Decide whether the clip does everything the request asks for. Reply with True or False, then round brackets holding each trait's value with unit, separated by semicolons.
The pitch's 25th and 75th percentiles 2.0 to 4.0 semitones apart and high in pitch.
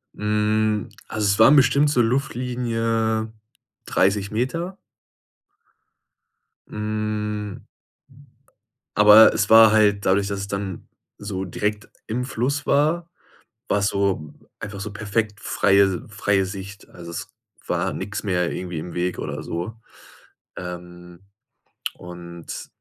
False (2.6 semitones; 105 Hz)